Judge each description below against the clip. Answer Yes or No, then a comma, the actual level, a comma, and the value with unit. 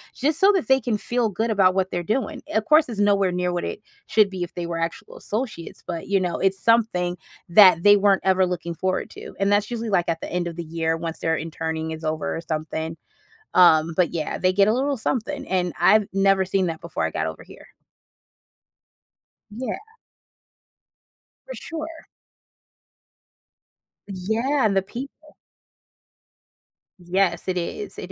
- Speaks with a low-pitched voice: No, high, 190 Hz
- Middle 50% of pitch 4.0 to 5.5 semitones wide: Yes, average, 4.4 semitones